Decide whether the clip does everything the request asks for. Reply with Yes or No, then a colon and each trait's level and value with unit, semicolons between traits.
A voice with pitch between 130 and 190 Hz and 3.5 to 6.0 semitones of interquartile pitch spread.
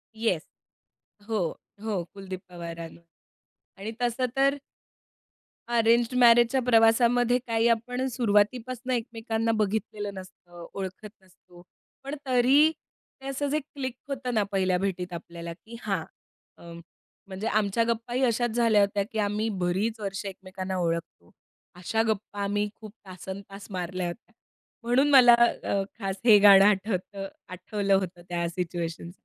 No: high, 210 Hz; average, 4.0 semitones